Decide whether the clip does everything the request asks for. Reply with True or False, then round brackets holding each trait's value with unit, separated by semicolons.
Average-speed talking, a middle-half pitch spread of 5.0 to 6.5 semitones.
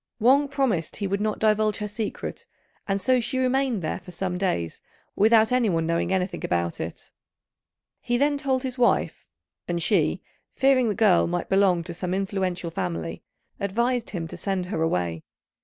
True (170 wpm; 5.4 semitones)